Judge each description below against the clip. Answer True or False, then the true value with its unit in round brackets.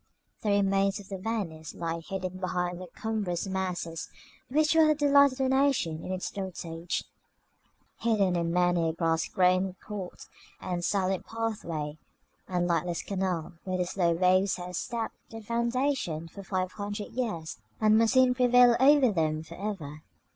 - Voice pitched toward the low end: False (190 Hz)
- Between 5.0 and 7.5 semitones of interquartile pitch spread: False (4.4 semitones)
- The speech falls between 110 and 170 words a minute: True (160 wpm)